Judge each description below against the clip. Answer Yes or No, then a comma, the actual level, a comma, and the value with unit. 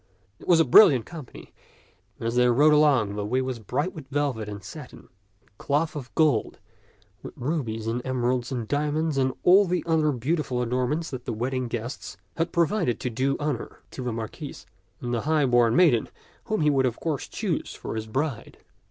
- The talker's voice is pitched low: Yes, low, 130 Hz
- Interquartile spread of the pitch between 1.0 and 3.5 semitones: No, average, 4.3 semitones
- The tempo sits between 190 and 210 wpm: Yes, average, 195 wpm